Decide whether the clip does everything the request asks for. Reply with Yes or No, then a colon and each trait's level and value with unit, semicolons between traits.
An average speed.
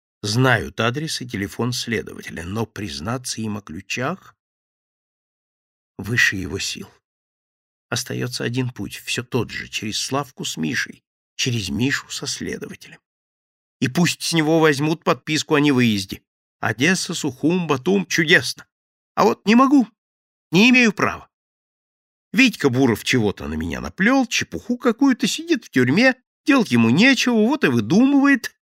Yes: average, 130 wpm